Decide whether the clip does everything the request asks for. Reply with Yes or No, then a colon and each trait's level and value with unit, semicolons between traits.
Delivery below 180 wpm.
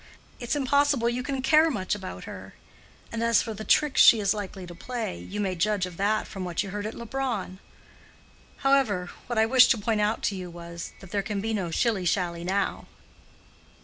No: fast, 205 wpm